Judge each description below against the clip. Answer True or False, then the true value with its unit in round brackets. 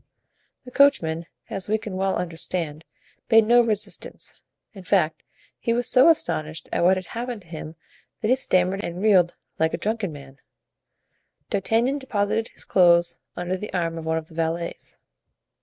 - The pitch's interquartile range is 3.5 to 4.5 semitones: False (5.1 semitones)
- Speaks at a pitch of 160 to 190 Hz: True (185 Hz)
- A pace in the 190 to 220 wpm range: False (165 wpm)